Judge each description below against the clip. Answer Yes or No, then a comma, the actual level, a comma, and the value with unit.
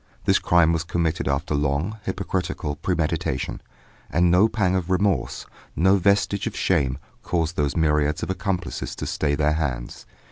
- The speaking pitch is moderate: No, very low, 85 Hz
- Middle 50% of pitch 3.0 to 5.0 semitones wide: Yes, average, 3.9 semitones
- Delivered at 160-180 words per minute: No, average, 150 wpm